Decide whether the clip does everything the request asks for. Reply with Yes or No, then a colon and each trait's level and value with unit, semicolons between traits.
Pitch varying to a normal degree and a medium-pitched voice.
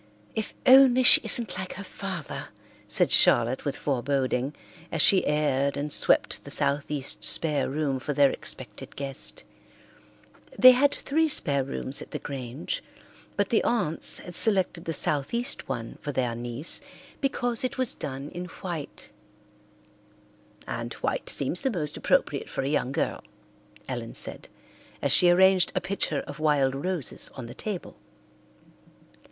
No: wide, 5.9 semitones; medium, 150 Hz